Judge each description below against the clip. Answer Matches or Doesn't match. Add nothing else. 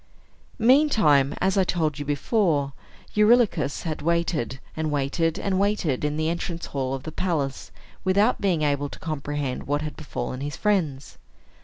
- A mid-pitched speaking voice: Matches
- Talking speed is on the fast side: Doesn't match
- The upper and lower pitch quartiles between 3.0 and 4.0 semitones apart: Doesn't match